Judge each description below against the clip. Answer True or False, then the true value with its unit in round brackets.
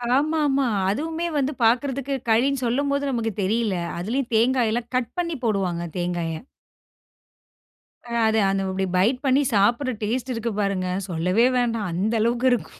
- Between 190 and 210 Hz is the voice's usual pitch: False (235 Hz)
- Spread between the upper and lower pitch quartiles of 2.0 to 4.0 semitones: False (4.9 semitones)